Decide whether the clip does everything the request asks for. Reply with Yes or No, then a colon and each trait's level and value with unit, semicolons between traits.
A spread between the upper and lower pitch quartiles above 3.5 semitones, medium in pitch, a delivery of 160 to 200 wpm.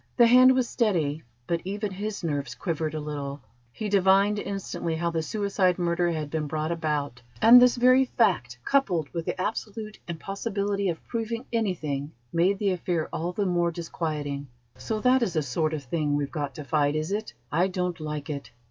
Yes: average, 5.1 semitones; medium, 170 Hz; average, 185 wpm